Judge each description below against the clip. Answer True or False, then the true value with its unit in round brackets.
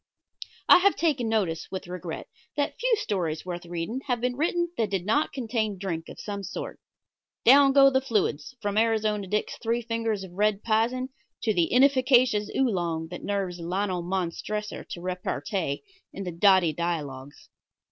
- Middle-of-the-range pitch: False (205 Hz)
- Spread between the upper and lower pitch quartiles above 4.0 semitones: True (5.3 semitones)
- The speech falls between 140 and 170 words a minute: True (160 wpm)